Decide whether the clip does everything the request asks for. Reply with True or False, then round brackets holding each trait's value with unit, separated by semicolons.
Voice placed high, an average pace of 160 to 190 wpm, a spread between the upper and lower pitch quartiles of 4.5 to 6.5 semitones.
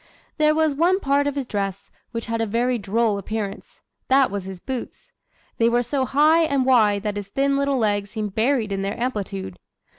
False (230 Hz; 200 wpm; 5.3 semitones)